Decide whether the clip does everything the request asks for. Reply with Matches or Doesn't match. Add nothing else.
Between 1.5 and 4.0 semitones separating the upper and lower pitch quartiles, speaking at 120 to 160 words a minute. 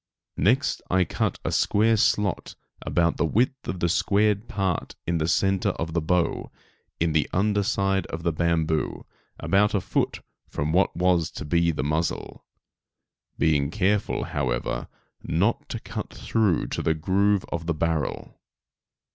Matches